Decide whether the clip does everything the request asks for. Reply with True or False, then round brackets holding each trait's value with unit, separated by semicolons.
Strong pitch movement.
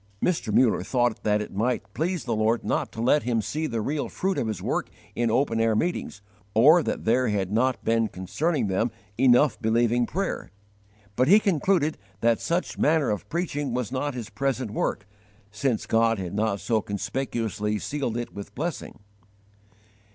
False (4.8 semitones)